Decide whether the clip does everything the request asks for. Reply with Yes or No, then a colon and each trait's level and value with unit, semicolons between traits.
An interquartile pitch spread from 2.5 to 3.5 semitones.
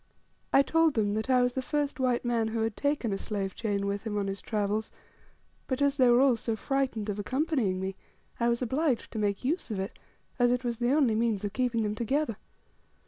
No: average, 3.9 semitones